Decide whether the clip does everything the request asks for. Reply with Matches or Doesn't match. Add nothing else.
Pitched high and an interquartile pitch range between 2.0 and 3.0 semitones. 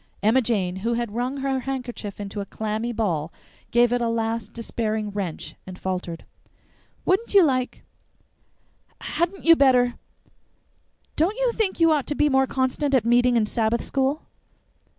Doesn't match